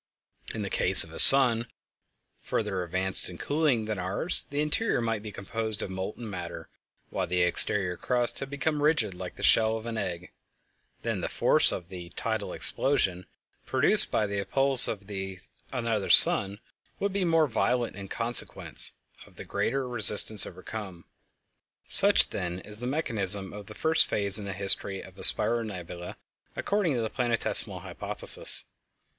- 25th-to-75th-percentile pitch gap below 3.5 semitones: No, average, 4.5 semitones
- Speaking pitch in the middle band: No, low, 110 Hz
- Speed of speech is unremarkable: Yes, average, 160 wpm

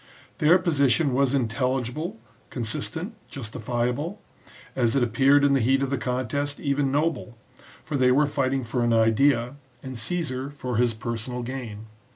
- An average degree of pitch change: Yes, average, 3.0 semitones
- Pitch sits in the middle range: No, low, 130 Hz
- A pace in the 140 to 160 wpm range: Yes, average, 155 wpm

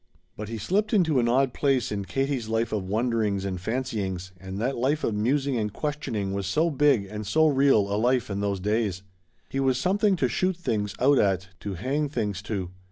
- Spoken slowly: No, fast, 205 wpm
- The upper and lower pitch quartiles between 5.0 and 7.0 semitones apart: Yes, average, 5.3 semitones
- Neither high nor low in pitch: No, low, 115 Hz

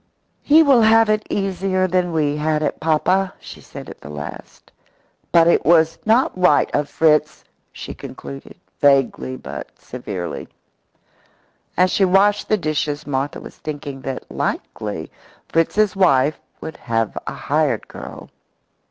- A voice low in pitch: No, medium, 160 Hz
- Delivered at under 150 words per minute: Yes, average, 140 wpm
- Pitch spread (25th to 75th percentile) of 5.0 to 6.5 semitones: Yes, wide, 5.4 semitones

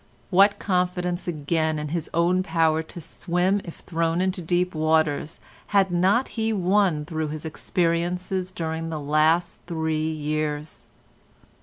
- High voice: No, medium, 170 Hz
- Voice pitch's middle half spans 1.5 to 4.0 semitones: Yes, narrow, 2.5 semitones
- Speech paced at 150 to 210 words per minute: No, slow, 135 wpm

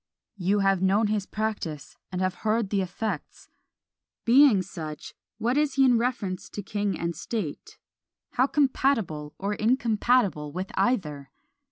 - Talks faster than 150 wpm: No, average, 140 wpm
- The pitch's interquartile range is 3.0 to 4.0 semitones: No, average, 4.4 semitones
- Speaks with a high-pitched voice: Yes, high, 205 Hz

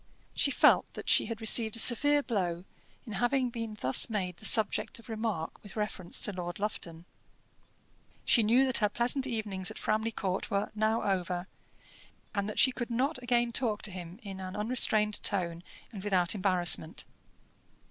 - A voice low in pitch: No, high, 210 Hz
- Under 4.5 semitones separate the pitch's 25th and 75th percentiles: Yes, average, 3.7 semitones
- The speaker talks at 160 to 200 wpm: Yes, average, 170 wpm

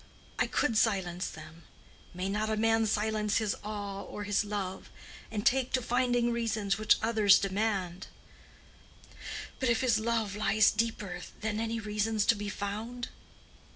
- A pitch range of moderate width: No, narrow, 2.1 semitones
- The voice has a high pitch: Yes, high, 215 Hz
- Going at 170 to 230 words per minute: No, average, 150 wpm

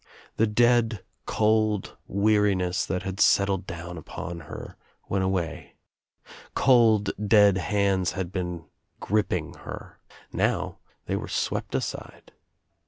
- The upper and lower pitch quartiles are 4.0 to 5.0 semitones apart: No, average, 2.8 semitones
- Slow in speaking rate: Yes, slow, 110 wpm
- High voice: No, low, 100 Hz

